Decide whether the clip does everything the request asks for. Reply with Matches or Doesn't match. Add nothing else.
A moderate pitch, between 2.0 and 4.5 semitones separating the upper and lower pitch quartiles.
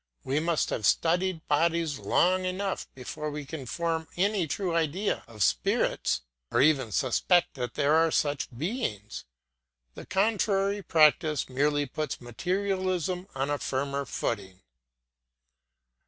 Doesn't match